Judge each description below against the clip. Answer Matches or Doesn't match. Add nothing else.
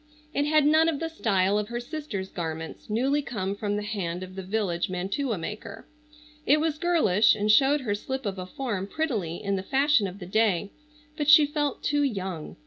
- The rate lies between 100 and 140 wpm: Doesn't match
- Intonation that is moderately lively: Doesn't match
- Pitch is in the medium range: Doesn't match